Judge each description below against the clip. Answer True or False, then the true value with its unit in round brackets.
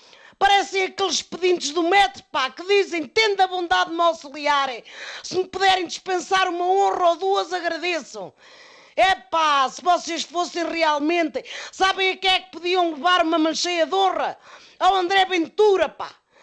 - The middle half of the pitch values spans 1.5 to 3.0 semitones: True (2.6 semitones)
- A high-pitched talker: True (360 Hz)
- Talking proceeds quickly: False (160 wpm)